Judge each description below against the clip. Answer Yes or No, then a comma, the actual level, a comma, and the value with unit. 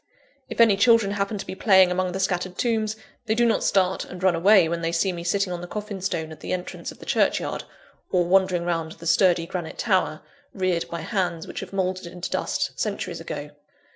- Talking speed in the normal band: No, fast, 215 wpm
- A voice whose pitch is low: No, medium, 185 Hz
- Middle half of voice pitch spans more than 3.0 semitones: No, narrow, 2.4 semitones